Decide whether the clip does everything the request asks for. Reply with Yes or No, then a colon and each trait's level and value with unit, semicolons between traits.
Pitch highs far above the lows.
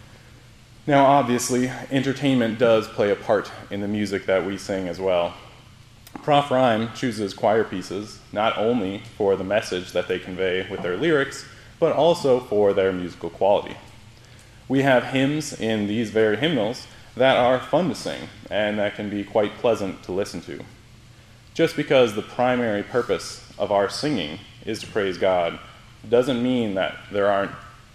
No: average, 3.6 semitones